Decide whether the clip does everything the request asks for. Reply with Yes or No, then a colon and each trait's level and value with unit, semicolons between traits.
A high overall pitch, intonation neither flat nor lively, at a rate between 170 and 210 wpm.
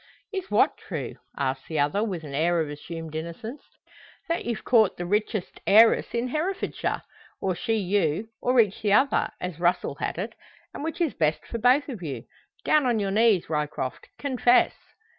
No: high, 205 Hz; wide, 6.8 semitones; average, 180 wpm